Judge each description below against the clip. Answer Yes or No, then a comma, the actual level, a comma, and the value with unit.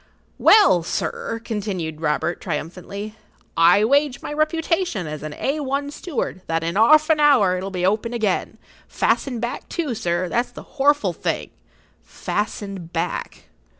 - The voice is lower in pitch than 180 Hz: No, high, 210 Hz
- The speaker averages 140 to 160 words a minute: Yes, average, 145 wpm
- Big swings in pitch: Yes, wide, 8.2 semitones